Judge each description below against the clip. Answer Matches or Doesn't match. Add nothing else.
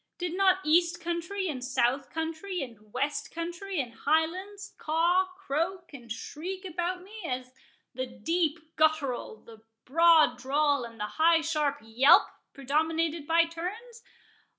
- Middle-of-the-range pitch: Doesn't match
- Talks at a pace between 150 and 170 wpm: Doesn't match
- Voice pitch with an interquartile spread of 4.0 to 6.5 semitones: Matches